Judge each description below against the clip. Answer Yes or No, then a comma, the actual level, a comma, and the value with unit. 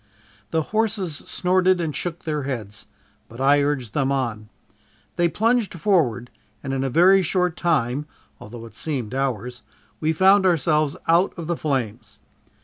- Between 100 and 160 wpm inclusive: Yes, average, 150 wpm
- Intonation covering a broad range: Yes, wide, 6.1 semitones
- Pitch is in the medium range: Yes, medium, 150 Hz